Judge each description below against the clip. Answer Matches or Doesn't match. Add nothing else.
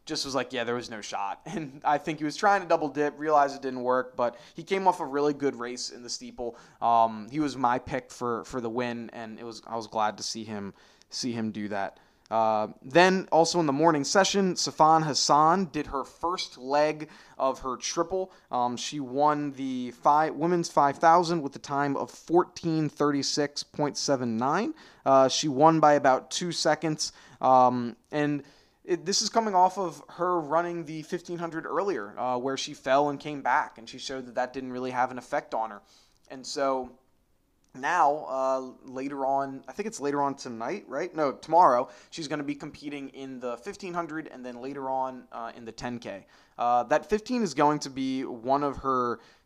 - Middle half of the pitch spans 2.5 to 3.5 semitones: Doesn't match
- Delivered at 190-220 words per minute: Matches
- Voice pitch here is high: Doesn't match